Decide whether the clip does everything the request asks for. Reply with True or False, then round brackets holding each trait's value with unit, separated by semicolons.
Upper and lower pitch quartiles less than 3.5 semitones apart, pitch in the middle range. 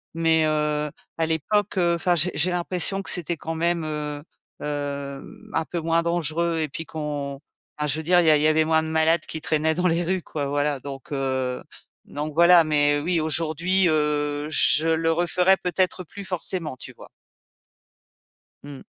True (2.5 semitones; 160 Hz)